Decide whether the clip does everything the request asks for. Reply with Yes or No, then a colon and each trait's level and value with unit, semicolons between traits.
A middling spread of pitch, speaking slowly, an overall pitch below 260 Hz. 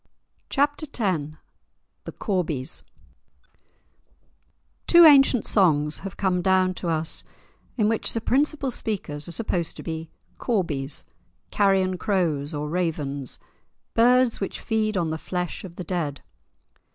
No: wide, 5.7 semitones; slow, 125 wpm; medium, 185 Hz